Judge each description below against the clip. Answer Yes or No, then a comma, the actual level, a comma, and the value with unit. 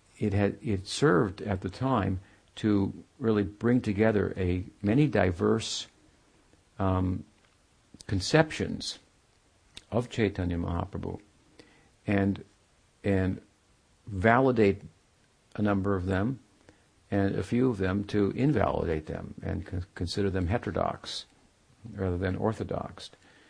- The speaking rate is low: Yes, slow, 105 wpm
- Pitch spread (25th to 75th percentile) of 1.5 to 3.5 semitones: Yes, narrow, 2.5 semitones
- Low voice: Yes, low, 100 Hz